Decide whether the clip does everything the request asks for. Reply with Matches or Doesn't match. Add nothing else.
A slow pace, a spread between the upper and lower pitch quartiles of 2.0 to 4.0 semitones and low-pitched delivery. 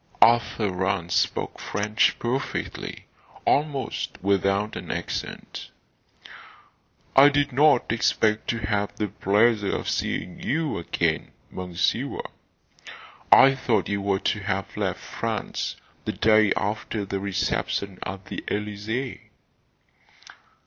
Matches